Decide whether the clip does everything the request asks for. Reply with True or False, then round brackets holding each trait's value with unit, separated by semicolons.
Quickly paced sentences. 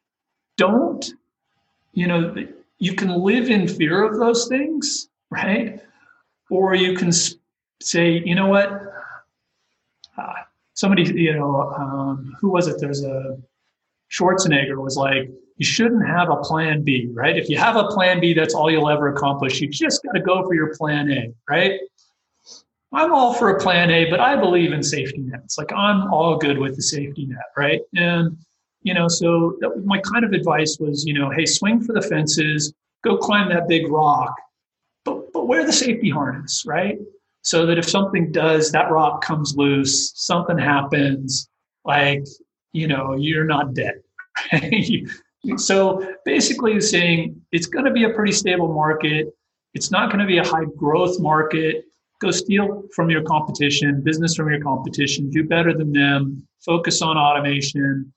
False (170 wpm)